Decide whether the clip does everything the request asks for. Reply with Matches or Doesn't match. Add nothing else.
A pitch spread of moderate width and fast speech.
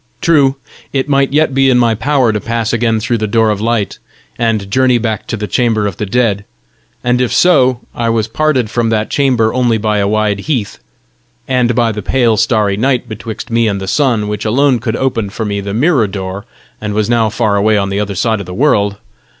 Matches